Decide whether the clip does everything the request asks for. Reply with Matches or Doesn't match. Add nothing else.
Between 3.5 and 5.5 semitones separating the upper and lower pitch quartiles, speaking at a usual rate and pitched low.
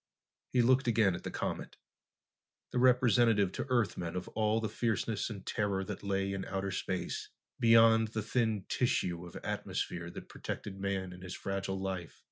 Doesn't match